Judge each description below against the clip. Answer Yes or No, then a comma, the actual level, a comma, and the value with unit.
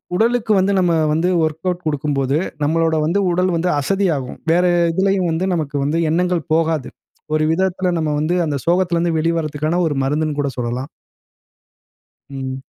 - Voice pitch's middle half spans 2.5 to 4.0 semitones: Yes, average, 3.3 semitones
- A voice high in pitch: No, medium, 165 Hz